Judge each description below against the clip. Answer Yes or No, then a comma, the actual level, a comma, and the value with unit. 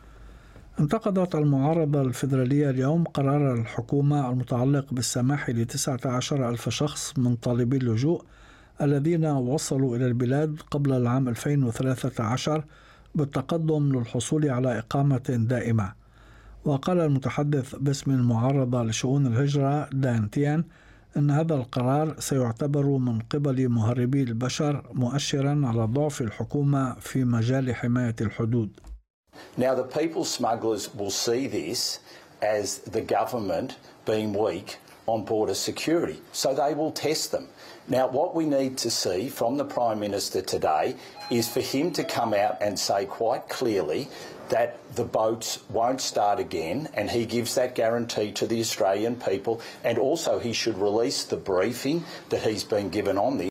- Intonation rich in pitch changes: No, average, 3.6 semitones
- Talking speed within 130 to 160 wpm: Yes, fast, 135 wpm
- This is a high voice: No, low, 130 Hz